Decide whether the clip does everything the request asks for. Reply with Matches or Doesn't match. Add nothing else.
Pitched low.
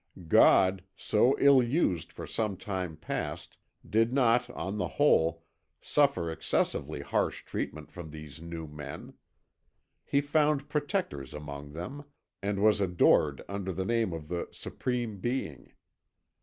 Matches